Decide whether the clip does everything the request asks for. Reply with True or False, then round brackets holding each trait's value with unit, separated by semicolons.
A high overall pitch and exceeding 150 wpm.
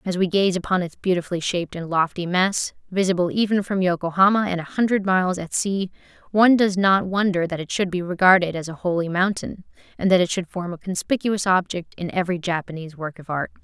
False (180 Hz; 205 wpm)